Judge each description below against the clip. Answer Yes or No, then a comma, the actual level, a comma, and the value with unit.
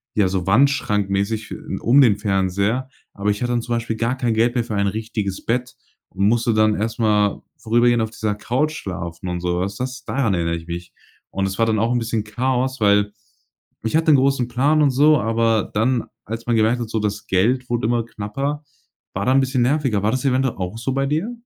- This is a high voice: No, low, 115 Hz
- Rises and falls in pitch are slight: No, average, 3.7 semitones